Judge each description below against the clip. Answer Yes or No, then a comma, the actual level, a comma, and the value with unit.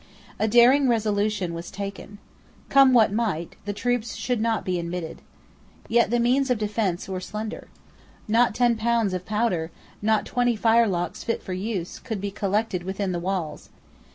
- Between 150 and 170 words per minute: Yes, average, 160 wpm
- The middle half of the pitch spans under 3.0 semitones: No, average, 3.8 semitones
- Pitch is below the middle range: No, high, 215 Hz